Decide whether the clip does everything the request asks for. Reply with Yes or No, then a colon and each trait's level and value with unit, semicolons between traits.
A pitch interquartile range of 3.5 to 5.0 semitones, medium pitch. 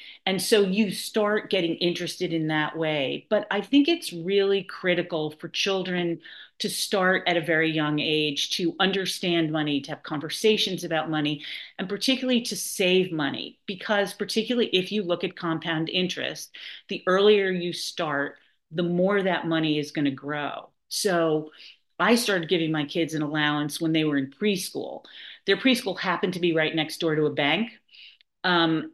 Yes: average, 4.1 semitones; medium, 175 Hz